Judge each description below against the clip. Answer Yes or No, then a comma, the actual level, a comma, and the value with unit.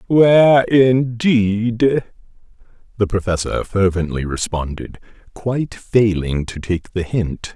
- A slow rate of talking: Yes, slow, 95 wpm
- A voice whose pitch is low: Yes, low, 105 Hz